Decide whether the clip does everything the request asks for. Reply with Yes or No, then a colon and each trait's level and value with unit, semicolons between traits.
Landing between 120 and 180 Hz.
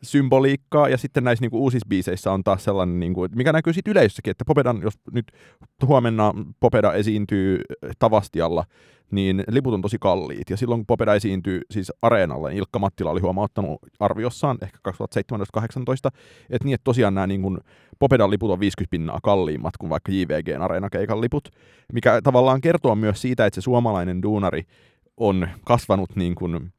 No: low, 105 Hz